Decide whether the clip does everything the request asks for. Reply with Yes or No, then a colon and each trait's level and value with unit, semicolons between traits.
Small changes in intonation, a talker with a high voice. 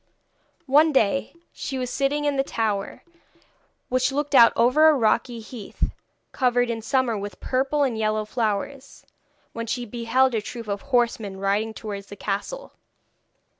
No: average, 3.9 semitones; high, 240 Hz